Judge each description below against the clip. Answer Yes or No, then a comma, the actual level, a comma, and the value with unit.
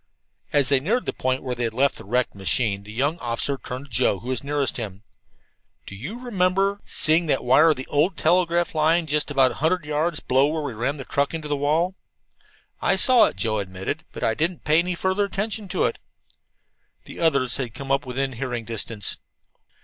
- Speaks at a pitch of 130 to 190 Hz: Yes, medium, 140 Hz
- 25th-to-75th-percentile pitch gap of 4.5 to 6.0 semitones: Yes, average, 5.0 semitones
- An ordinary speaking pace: No, fast, 220 wpm